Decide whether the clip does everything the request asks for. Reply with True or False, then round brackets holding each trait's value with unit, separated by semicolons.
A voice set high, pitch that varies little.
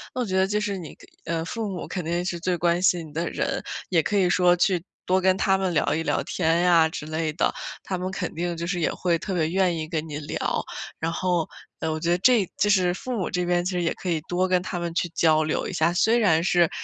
False (175 Hz; 2.1 semitones)